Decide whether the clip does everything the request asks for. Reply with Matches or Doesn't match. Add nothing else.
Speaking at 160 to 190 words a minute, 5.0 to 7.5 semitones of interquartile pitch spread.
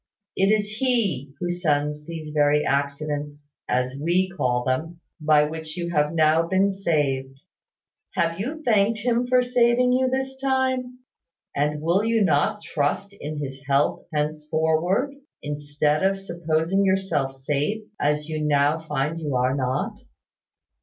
Doesn't match